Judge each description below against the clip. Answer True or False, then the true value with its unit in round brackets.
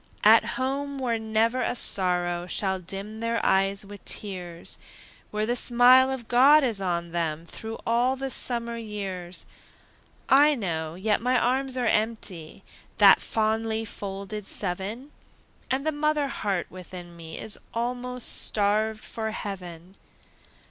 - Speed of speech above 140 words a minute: False (135 wpm)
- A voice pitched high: True (220 Hz)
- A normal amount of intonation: True (4.7 semitones)